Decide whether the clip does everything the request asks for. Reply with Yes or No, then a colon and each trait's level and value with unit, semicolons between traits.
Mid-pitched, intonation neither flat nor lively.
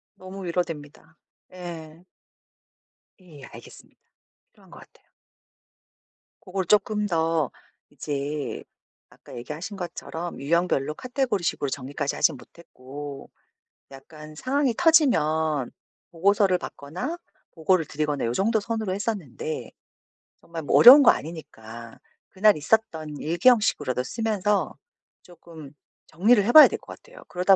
No: medium, 170 Hz; wide, 5.7 semitones